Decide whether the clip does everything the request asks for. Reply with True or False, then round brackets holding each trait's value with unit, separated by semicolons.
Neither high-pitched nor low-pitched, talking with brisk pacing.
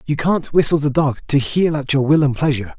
True (145 Hz; 260 wpm)